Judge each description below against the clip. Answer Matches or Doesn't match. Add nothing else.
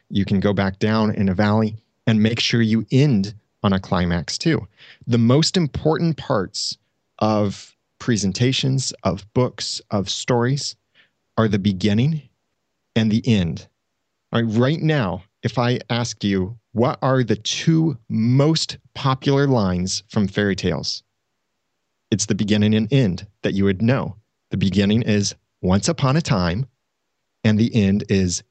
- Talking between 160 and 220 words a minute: Doesn't match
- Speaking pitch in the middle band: Doesn't match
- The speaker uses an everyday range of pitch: Matches